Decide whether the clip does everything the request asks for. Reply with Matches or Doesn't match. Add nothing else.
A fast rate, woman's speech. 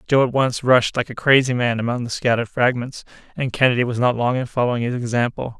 Doesn't match